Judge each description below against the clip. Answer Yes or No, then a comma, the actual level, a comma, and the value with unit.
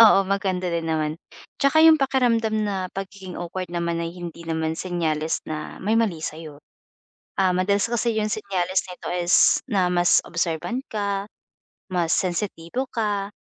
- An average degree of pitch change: Yes, average, 3.6 semitones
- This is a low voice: No, medium, 185 Hz